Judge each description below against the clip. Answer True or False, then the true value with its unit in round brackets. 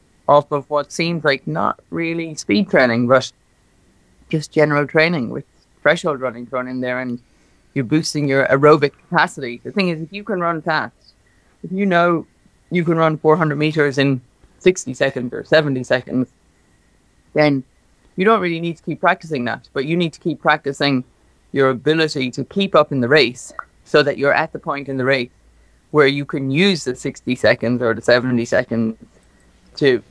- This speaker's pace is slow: False (180 wpm)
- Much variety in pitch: False (4.1 semitones)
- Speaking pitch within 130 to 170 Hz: True (140 Hz)